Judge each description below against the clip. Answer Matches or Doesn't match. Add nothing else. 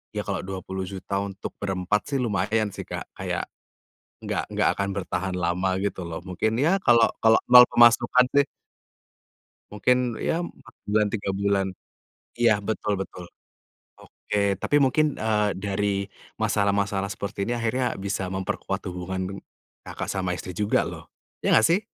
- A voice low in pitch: Matches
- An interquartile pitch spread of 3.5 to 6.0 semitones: Doesn't match